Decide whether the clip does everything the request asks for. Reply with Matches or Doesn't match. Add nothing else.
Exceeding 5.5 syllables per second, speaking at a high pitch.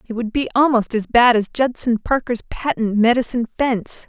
Doesn't match